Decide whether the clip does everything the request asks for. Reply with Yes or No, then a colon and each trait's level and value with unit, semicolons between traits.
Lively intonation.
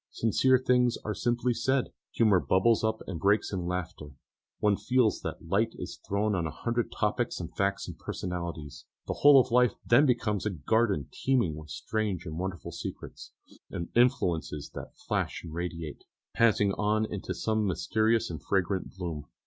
No: average, 5.0 semitones